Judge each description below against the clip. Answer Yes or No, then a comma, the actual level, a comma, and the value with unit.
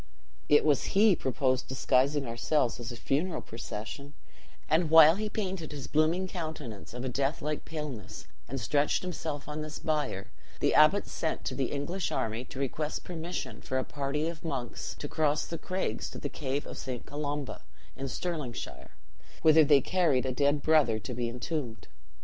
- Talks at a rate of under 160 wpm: No, average, 175 wpm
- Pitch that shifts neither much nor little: Yes, average, 3.5 semitones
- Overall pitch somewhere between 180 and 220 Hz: No, medium, 145 Hz